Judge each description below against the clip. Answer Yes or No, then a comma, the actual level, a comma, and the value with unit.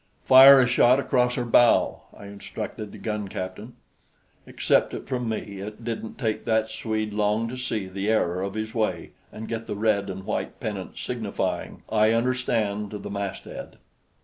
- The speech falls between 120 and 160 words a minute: No, average, 175 wpm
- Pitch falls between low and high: No, low, 110 Hz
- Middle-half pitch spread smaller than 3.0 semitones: Yes, narrow, 2.6 semitones